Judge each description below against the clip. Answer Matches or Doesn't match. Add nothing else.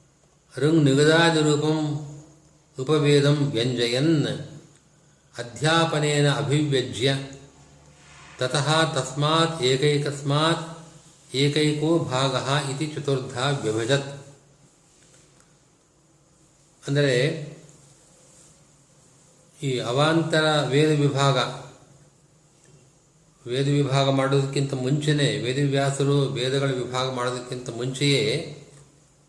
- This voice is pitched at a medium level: Matches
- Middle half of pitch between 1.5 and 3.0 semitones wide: Matches